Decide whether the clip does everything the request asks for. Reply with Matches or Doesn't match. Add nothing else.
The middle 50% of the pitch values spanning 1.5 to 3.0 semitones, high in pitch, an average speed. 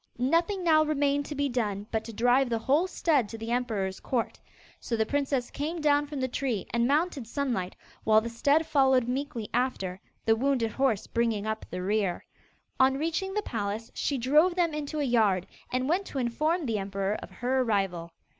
Doesn't match